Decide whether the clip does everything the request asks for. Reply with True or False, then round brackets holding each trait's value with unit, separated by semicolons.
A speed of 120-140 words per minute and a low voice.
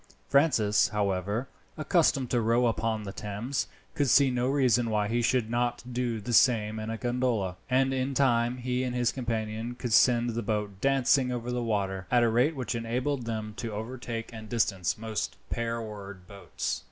False (180 wpm; 115 Hz)